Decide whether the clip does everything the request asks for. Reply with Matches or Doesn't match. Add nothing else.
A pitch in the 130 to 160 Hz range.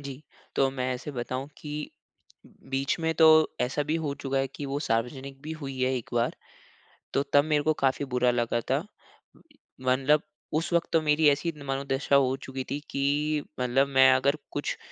Matches